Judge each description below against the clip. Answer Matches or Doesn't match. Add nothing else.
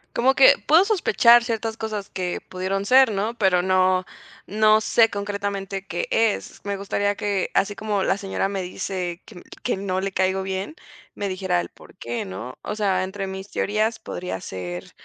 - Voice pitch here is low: Doesn't match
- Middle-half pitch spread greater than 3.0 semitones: Doesn't match